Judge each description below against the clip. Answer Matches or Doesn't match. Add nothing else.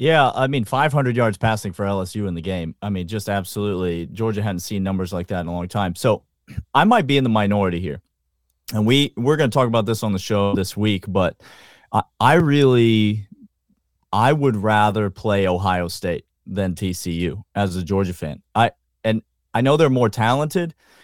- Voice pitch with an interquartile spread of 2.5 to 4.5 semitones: Matches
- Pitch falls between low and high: Doesn't match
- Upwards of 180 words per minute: Matches